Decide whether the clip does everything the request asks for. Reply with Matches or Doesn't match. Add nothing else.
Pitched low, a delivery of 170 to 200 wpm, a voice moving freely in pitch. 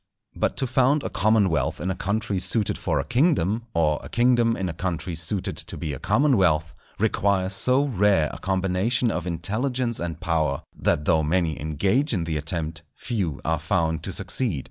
Matches